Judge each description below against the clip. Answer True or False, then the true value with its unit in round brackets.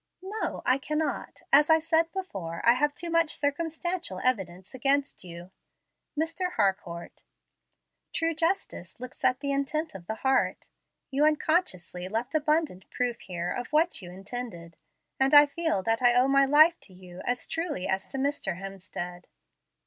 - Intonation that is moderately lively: False (8.5 semitones)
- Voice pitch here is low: False (265 Hz)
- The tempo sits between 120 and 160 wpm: True (155 wpm)